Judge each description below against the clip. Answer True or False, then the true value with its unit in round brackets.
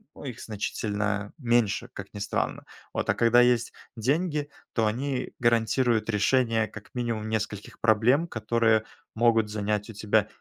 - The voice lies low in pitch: True (115 Hz)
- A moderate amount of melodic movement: False (2.3 semitones)